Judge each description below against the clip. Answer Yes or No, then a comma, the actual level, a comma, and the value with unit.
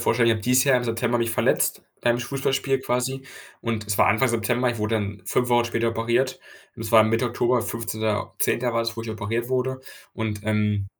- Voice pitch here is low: Yes, low, 115 Hz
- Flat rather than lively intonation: Yes, narrow, 2.1 semitones